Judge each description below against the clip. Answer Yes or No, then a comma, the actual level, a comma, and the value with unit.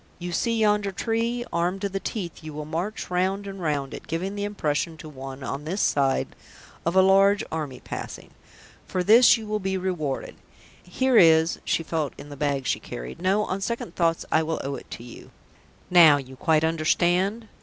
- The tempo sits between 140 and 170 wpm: No, average, 195 wpm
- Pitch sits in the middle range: Yes, medium, 175 Hz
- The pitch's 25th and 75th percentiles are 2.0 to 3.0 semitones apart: No, average, 4.5 semitones